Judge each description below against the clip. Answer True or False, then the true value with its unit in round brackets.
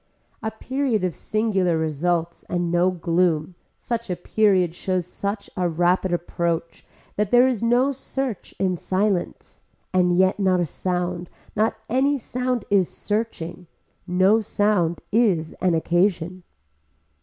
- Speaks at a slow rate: True (130 wpm)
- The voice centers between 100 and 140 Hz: False (185 Hz)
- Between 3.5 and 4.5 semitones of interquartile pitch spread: True (3.8 semitones)